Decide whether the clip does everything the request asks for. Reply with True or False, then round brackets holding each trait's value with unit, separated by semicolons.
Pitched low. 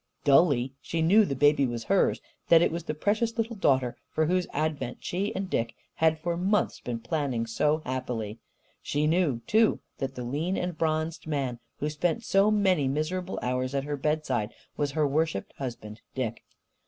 False (150 Hz)